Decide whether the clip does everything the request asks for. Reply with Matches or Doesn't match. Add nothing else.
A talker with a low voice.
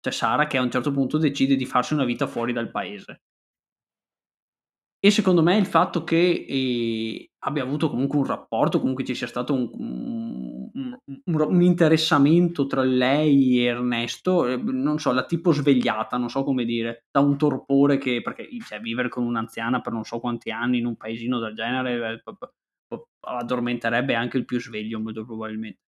Matches